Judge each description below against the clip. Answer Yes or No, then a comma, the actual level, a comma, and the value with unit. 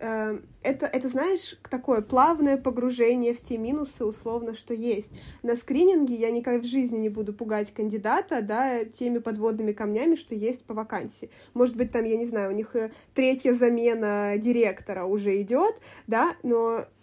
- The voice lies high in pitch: Yes, high, 235 Hz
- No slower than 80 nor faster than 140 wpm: No, fast, 160 wpm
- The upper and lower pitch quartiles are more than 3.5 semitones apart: No, average, 3.0 semitones